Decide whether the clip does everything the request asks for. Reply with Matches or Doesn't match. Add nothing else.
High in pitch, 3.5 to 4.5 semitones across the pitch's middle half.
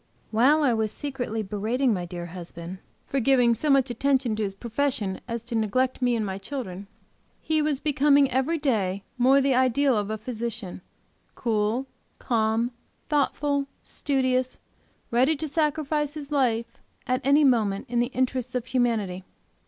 Matches